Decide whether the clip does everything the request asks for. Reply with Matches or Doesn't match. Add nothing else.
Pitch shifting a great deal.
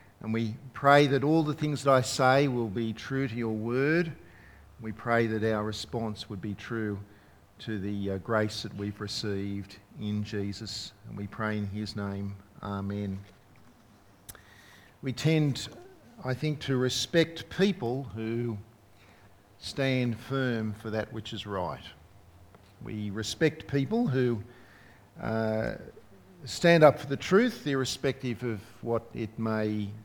Doesn't match